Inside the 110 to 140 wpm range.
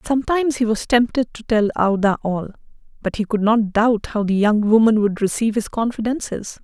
No: average, 190 wpm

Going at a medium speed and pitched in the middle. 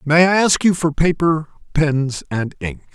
Yes: average, 185 wpm; medium, 155 Hz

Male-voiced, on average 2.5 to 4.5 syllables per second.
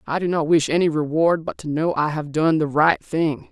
No: male; 5.1 syllables/s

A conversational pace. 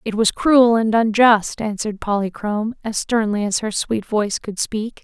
Yes: average, 180 wpm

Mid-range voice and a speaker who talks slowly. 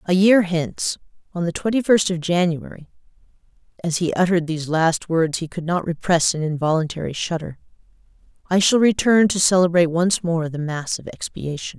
No: medium, 175 Hz; average, 170 wpm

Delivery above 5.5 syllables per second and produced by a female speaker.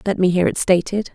Yes: 5.9 syllables/s; female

